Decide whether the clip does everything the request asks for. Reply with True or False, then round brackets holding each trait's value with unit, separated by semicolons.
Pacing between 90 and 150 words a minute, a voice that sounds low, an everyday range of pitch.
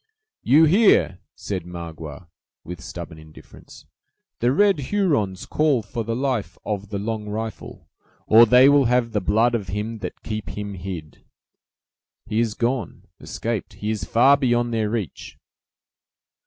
True (140 wpm; 110 Hz; 3.9 semitones)